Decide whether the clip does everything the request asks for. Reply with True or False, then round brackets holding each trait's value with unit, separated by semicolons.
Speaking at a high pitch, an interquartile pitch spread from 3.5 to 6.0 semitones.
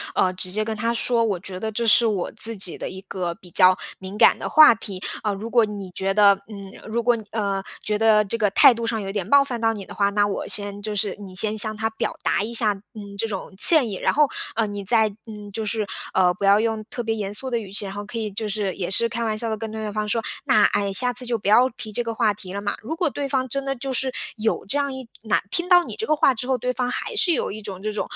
False (215 Hz; 2.7 semitones)